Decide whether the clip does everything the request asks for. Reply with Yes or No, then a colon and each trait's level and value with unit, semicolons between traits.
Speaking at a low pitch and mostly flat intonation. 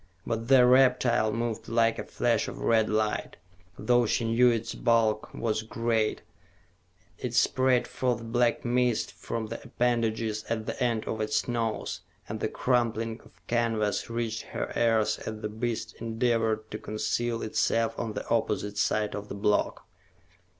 Yes: low, 115 Hz; narrow, 1.6 semitones